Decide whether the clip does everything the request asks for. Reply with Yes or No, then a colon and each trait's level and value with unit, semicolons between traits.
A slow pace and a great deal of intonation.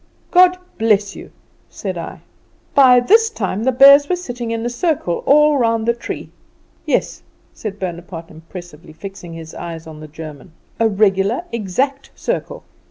No: average, 155 wpm; wide, 7.1 semitones